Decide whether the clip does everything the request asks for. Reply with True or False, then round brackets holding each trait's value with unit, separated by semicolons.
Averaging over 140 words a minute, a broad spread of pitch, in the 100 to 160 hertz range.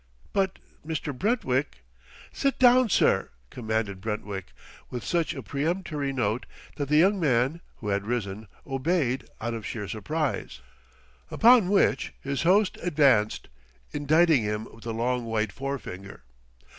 False (135 wpm; 6.9 semitones; 135 Hz)